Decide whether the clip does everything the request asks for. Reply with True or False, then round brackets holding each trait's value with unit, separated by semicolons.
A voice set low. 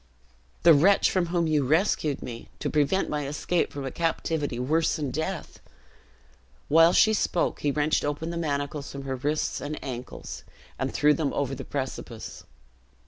False (150 Hz)